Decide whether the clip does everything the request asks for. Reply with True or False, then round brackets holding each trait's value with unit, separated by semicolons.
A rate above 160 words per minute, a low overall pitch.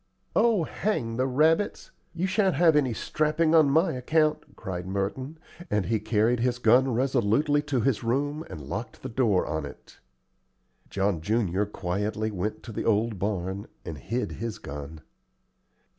False (155 wpm; 115 Hz)